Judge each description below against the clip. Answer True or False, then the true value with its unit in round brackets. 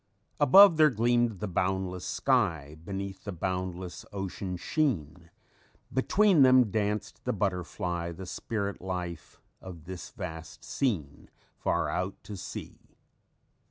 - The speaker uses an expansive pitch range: False (4.4 semitones)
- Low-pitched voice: True (95 Hz)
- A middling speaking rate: False (125 wpm)